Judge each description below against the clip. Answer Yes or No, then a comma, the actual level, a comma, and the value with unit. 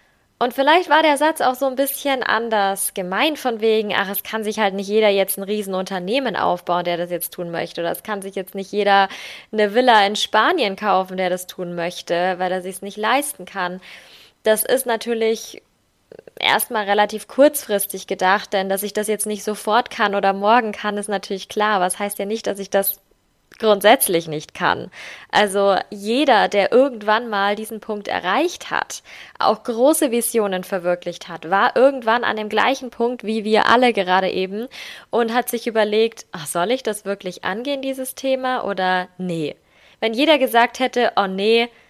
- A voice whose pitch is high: Yes, high, 210 Hz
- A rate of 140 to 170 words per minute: No, average, 185 wpm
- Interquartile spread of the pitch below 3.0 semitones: No, average, 3.5 semitones